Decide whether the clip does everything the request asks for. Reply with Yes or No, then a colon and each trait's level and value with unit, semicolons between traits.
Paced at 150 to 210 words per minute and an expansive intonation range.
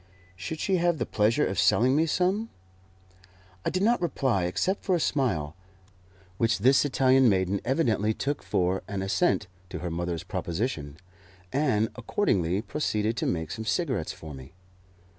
Yes: average, 155 wpm; wide, 8.3 semitones